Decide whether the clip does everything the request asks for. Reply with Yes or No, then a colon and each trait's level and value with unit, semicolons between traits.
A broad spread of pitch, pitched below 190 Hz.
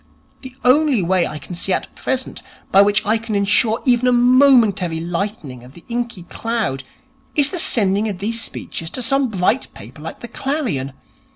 No: wide, 5.7 semitones; high, 215 Hz